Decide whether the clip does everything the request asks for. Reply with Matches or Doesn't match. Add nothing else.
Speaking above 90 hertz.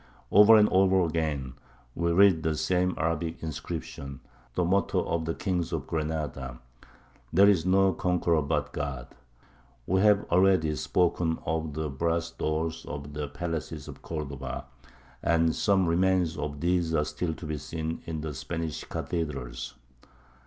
Doesn't match